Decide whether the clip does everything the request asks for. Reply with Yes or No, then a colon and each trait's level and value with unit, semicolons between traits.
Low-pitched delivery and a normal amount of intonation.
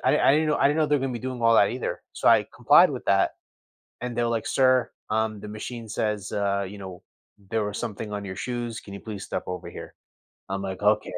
Yes: low, 110 Hz; average, 3.4 semitones